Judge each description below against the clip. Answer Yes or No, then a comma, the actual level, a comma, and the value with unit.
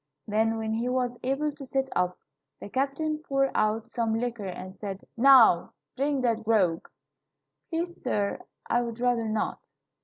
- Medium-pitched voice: No, high, 235 Hz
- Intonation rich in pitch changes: No, average, 3.8 semitones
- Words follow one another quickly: No, average, 155 wpm